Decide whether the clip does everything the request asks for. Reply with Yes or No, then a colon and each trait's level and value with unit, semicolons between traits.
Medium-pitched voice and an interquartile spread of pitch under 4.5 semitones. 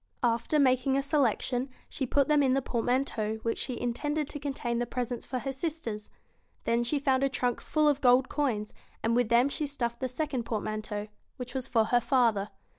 No: very high, 250 Hz; average, 2.8 semitones